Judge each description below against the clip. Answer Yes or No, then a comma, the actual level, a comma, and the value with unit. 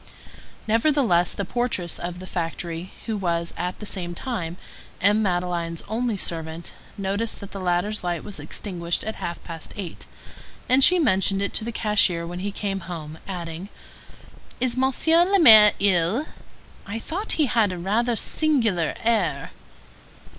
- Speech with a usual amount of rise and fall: Yes, average, 4.7 semitones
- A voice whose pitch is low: No, high, 195 Hz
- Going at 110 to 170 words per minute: Yes, average, 155 wpm